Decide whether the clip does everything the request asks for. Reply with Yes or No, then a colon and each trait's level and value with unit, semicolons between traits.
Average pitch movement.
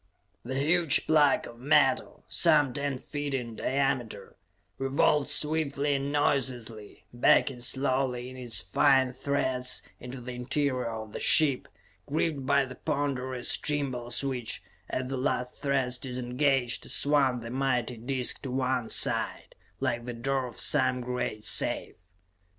No: narrow, 2.2 semitones